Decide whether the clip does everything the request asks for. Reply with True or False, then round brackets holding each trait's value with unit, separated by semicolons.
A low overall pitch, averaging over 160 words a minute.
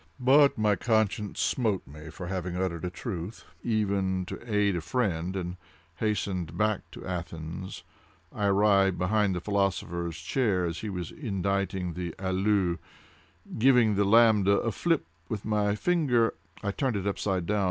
False (100 Hz; 150 wpm)